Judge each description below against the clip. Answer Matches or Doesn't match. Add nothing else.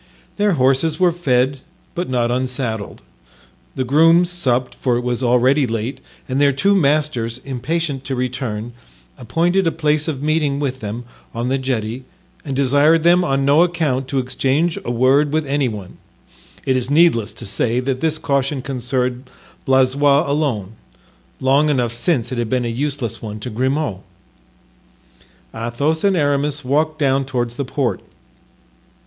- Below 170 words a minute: Matches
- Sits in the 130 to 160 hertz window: Matches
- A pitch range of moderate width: Matches